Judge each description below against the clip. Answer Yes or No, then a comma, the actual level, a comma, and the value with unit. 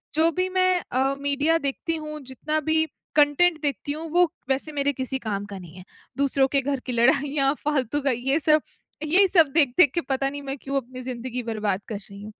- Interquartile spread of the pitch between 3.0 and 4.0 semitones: Yes, average, 3.3 semitones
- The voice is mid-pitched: No, very high, 275 Hz